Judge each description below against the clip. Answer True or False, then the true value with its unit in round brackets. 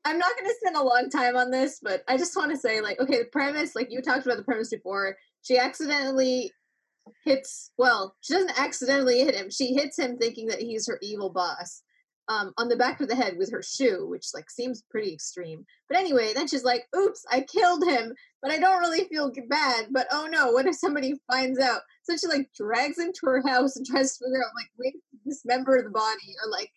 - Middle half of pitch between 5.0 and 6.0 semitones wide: False (3.8 semitones)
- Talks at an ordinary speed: False (235 wpm)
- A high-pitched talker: True (260 Hz)